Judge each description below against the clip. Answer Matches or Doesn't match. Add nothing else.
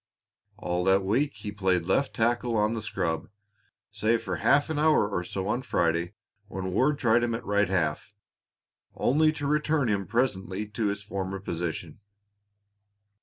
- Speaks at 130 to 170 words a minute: Matches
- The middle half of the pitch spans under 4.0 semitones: Doesn't match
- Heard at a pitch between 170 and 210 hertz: Doesn't match